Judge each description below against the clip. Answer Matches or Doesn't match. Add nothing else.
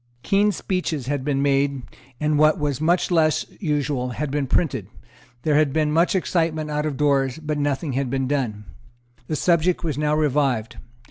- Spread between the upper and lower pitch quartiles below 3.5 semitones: Matches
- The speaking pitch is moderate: Matches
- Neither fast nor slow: Matches